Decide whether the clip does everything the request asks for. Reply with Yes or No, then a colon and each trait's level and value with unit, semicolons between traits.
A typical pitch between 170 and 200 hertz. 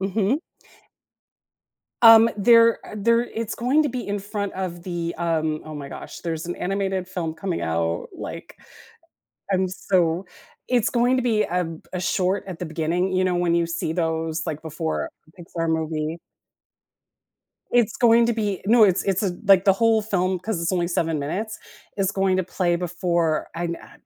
Yes: medium, 185 Hz